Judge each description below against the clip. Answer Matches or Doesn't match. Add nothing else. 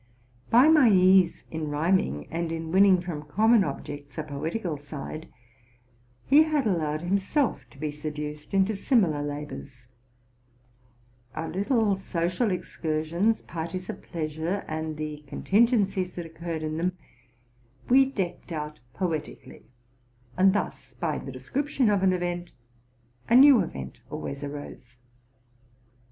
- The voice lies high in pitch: Doesn't match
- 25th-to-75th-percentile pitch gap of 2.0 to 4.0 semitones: Doesn't match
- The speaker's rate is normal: Doesn't match